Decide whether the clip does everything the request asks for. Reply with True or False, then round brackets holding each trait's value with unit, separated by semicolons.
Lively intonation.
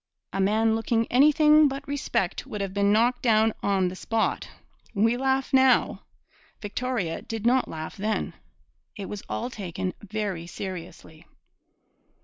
False (4.5 semitones)